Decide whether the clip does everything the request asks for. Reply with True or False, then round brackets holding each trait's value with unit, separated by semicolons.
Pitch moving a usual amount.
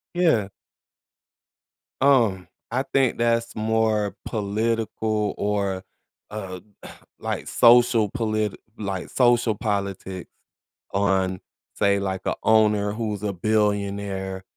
False (2.3 semitones)